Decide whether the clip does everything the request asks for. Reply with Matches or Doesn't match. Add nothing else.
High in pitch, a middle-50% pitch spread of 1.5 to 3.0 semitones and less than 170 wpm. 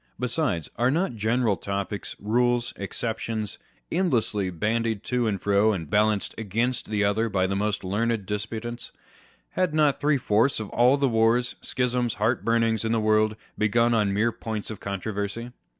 Doesn't match